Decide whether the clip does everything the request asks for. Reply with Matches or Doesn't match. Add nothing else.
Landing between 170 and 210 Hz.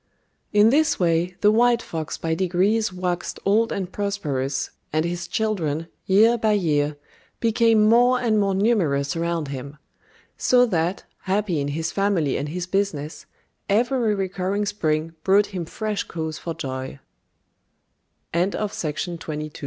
Matches